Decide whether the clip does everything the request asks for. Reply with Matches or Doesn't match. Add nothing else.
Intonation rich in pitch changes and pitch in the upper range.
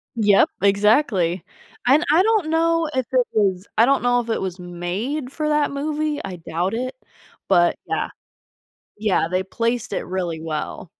Matches